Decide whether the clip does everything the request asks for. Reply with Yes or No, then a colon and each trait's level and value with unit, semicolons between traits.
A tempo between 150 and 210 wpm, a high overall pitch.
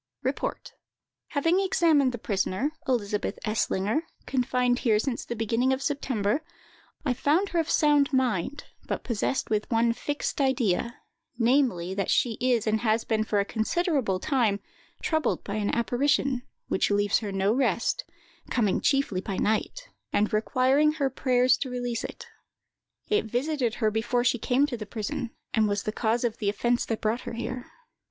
Yes: average, 165 wpm; high, 240 Hz